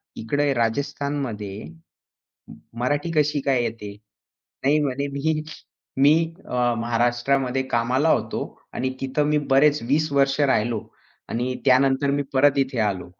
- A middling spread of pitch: Yes, average, 3.0 semitones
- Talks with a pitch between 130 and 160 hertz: Yes, low, 135 Hz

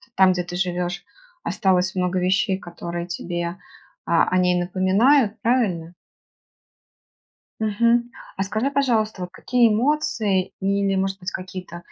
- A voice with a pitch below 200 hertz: Yes, high, 190 Hz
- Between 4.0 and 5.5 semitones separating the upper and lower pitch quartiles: No, average, 3.4 semitones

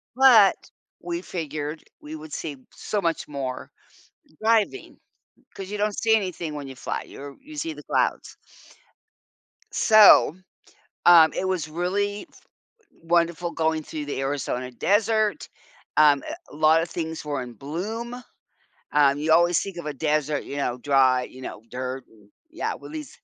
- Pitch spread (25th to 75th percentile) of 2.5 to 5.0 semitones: No, wide, 5.6 semitones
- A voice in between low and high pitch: Yes, medium, 160 Hz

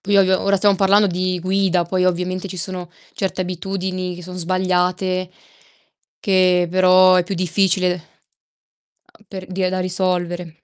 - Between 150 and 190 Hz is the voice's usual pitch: Yes, medium, 185 Hz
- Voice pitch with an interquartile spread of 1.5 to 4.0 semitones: No, narrow, 0.9 semitones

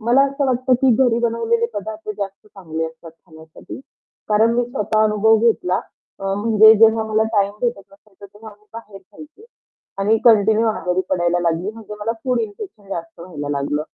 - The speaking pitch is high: Yes, high, 215 Hz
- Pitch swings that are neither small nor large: Yes, average, 3.3 semitones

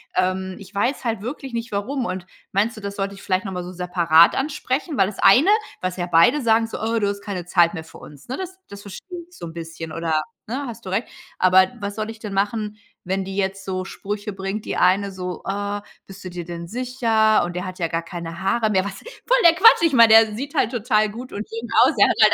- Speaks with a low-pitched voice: No, high, 200 Hz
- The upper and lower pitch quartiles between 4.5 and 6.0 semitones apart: No, average, 3.7 semitones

